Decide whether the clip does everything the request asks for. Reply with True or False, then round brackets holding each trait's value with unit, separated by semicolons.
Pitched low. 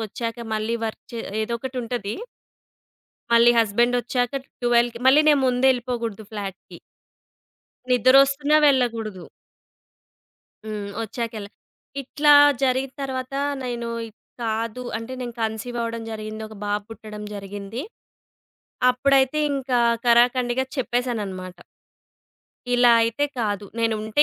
False (235 Hz)